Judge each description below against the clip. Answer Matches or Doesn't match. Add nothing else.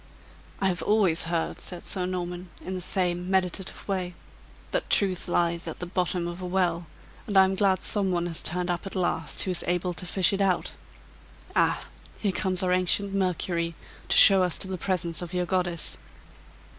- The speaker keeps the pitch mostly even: Matches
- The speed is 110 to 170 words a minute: Doesn't match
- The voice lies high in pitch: Doesn't match